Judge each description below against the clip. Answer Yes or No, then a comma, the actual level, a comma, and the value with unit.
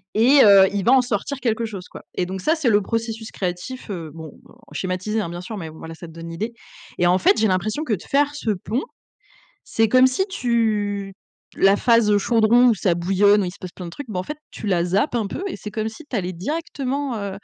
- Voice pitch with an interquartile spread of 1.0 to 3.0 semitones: No, average, 4.6 semitones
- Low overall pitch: No, high, 210 Hz